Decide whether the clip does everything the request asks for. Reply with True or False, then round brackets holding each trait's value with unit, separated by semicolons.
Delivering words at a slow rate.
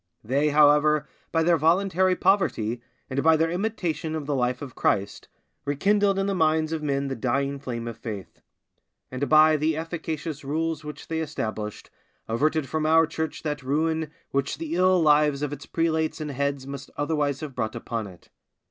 False (175 wpm)